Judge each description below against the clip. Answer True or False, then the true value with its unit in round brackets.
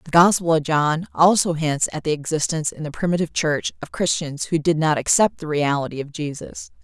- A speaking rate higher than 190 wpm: True (200 wpm)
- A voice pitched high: False (160 Hz)